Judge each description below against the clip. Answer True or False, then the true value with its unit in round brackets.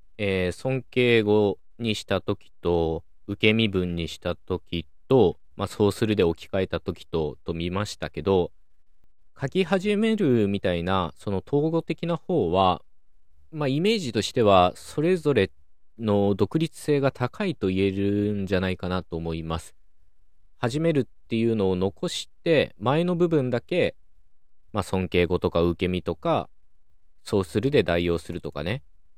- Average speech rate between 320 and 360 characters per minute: False (275 characters per minute)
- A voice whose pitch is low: True (95 Hz)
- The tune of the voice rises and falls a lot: True (6.3 semitones)